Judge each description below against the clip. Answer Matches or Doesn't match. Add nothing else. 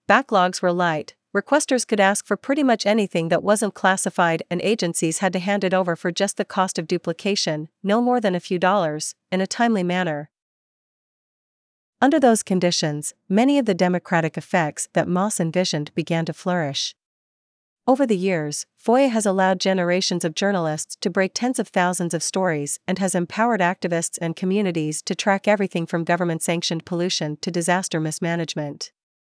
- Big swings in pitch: Doesn't match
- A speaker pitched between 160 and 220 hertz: Matches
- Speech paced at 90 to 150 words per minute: Doesn't match